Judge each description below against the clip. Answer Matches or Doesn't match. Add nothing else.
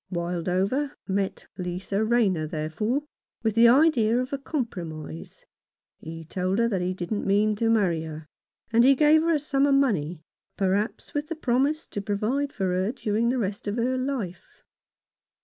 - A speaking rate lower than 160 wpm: Doesn't match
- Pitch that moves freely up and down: Matches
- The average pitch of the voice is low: Doesn't match